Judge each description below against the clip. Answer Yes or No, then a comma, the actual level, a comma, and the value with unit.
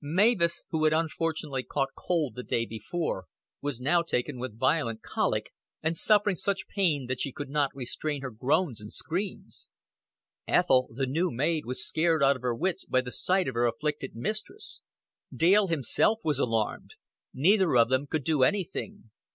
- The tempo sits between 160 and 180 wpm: Yes, average, 170 wpm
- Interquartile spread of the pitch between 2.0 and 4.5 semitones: No, average, 5.2 semitones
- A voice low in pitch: No, medium, 150 Hz